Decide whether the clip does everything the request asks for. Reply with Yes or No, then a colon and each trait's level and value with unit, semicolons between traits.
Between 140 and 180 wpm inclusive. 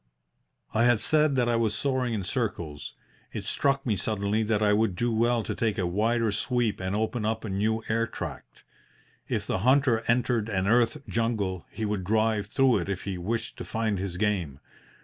No: average, 195 wpm